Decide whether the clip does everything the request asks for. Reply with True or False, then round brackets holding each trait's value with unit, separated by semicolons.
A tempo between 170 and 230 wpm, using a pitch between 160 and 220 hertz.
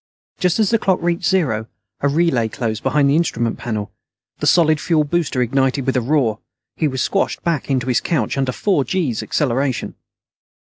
False (180 wpm; 140 Hz)